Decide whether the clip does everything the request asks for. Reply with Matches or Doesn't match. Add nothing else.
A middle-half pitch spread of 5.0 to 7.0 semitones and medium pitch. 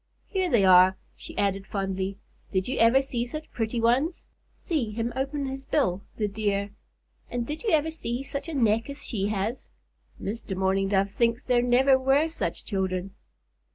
Doesn't match